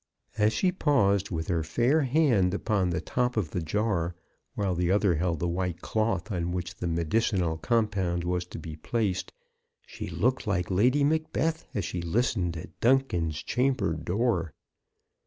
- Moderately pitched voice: No, very low, 95 Hz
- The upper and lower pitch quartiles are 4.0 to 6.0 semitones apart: Yes, wide, 5.4 semitones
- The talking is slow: No, average, 160 wpm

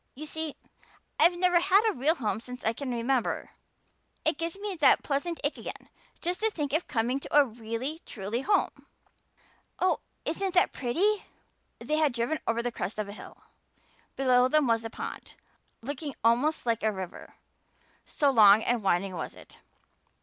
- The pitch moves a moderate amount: No, wide, 5.9 semitones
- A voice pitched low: No, very high, 270 Hz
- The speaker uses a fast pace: No, average, 170 wpm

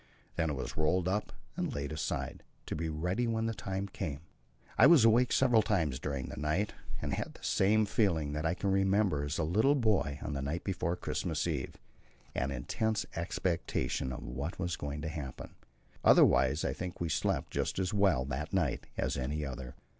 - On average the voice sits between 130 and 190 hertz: No, very low, 85 Hz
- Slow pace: No, average, 190 wpm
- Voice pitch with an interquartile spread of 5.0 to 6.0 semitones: Yes, wide, 5.5 semitones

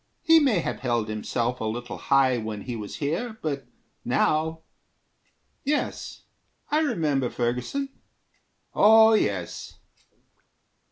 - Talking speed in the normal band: No, slow, 110 wpm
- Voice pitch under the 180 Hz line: Yes, low, 135 Hz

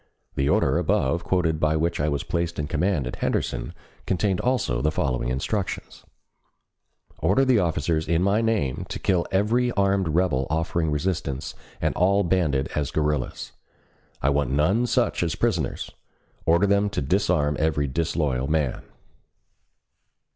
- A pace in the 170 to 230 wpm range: No, average, 145 wpm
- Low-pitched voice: Yes, very low, 80 Hz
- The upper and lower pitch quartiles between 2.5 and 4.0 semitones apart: No, average, 4.7 semitones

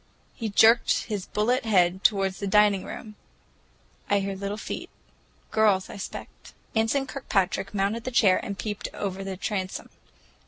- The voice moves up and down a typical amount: No, narrow, 2.2 semitones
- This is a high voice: Yes, high, 205 Hz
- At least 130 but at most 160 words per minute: Yes, average, 145 wpm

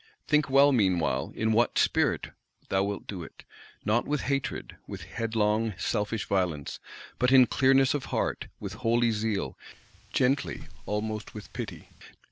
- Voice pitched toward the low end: Yes, low, 110 Hz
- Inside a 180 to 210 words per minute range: No, average, 140 wpm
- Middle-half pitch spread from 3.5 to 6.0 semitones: Yes, average, 4.0 semitones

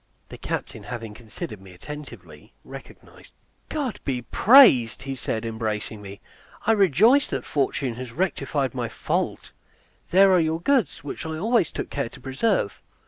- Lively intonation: Yes, wide, 8.7 semitones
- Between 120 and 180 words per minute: Yes, average, 155 wpm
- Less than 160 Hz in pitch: Yes, medium, 140 Hz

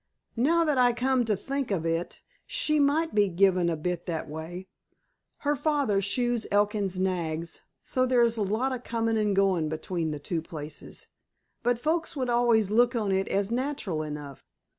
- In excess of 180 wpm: No, average, 175 wpm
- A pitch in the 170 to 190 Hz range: No, high, 210 Hz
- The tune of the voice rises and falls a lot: Yes, wide, 6.0 semitones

